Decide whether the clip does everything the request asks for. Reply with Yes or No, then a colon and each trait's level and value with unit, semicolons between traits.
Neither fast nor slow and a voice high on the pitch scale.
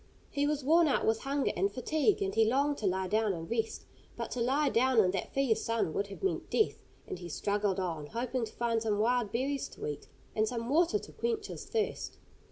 No: fast, 225 wpm; high, 235 Hz